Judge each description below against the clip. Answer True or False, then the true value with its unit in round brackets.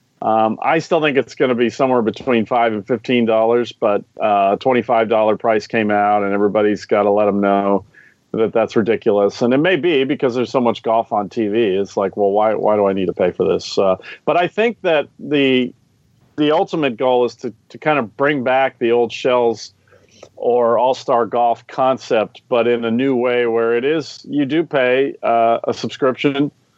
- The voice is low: True (120 Hz)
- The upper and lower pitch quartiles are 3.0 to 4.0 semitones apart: True (3.7 semitones)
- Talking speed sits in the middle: False (210 wpm)